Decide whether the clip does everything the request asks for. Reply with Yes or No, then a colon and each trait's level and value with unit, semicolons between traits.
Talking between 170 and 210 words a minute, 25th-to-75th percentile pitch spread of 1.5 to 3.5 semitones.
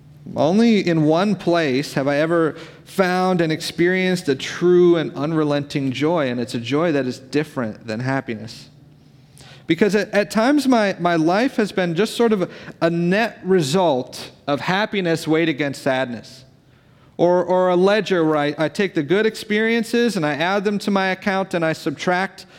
No: average, 175 wpm; average, 4.9 semitones